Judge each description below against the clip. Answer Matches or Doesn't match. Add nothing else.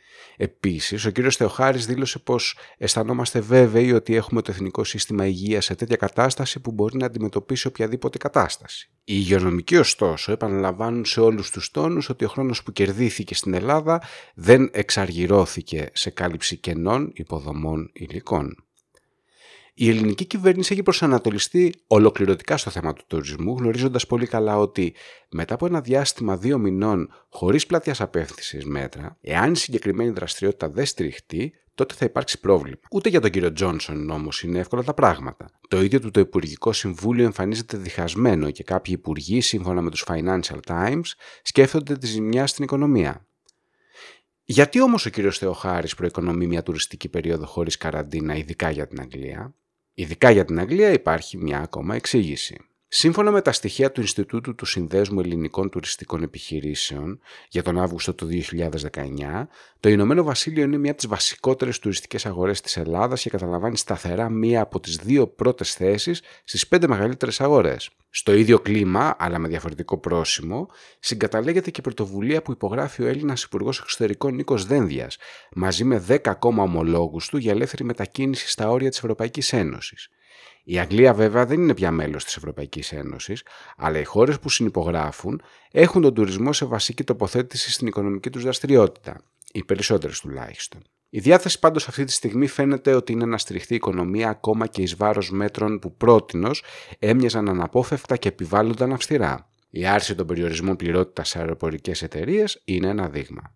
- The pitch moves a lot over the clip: Matches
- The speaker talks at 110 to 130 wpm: Doesn't match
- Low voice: Matches